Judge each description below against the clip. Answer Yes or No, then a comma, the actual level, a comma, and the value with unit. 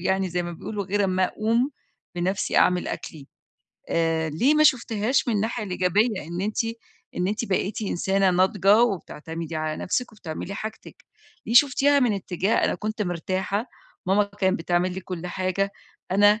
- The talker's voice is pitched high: Yes, high, 195 Hz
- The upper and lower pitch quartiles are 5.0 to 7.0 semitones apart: No, average, 3.2 semitones